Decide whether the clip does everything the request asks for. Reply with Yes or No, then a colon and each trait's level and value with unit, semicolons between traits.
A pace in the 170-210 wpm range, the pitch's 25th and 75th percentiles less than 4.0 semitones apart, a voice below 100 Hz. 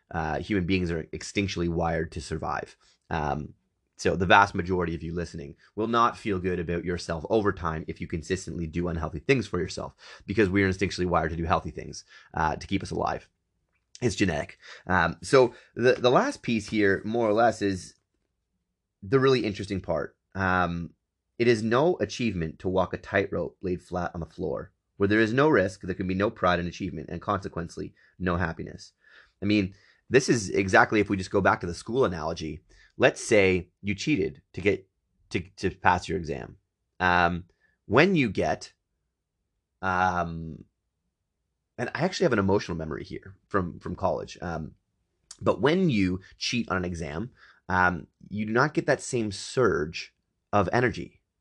Yes: average, 175 wpm; average, 2.9 semitones; very low, 90 Hz